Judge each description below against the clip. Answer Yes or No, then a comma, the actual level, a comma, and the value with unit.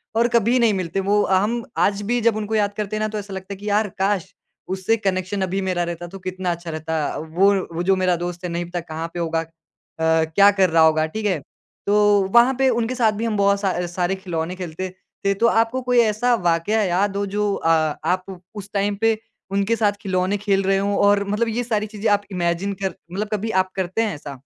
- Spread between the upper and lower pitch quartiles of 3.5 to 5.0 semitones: No, average, 3.1 semitones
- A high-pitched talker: Yes, high, 195 Hz